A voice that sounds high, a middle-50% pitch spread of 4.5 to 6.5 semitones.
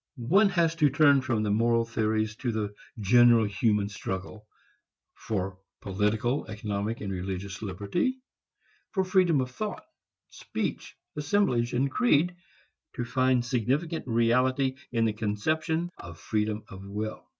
No: low, 115 Hz; average, 5.1 semitones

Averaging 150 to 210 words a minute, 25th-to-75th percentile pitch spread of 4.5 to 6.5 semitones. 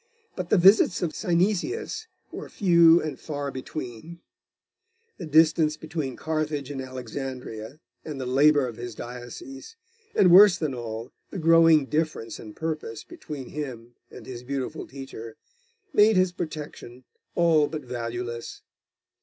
No: slow, 135 wpm; average, 5.1 semitones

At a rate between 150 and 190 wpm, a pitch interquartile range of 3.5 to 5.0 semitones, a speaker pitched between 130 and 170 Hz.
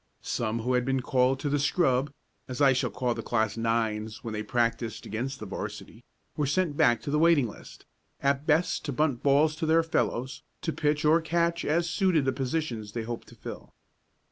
No: average, 200 wpm; average, 4.6 semitones; low, 135 Hz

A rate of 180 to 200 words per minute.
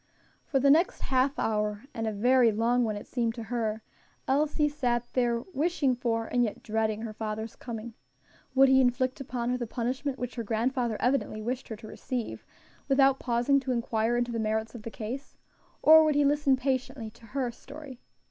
Yes: average, 190 wpm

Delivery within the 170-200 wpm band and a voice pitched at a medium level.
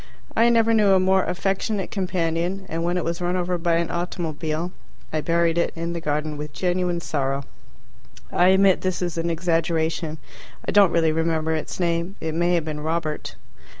Yes: average, 185 wpm; medium, 170 Hz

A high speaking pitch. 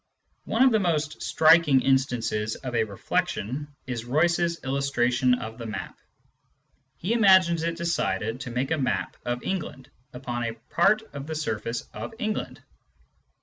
No: low, 135 Hz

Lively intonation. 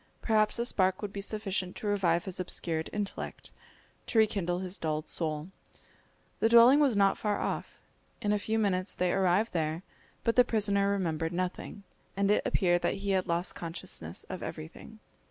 No: average, 3.1 semitones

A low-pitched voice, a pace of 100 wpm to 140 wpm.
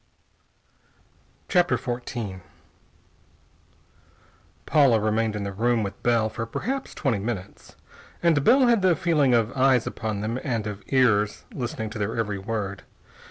Yes: low, 115 Hz; slow, 135 wpm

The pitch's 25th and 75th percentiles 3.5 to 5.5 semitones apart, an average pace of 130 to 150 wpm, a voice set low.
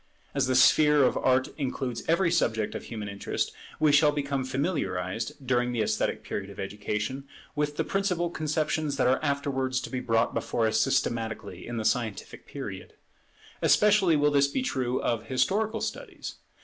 No: average, 4.4 semitones; average, 165 wpm; low, 130 Hz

